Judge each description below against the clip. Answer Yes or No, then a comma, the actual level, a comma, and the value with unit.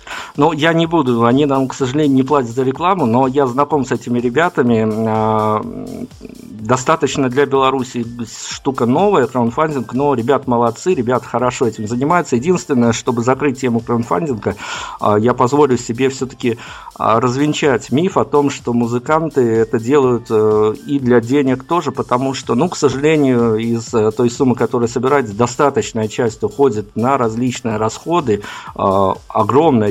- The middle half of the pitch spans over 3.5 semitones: No, average, 3.2 semitones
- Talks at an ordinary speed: Yes, average, 140 wpm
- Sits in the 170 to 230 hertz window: No, low, 125 Hz